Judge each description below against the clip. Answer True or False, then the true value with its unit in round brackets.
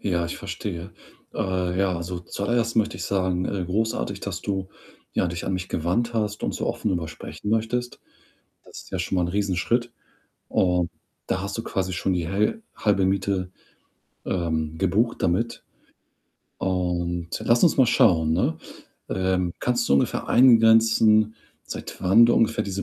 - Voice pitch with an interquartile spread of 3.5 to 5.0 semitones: True (4.0 semitones)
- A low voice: True (95 Hz)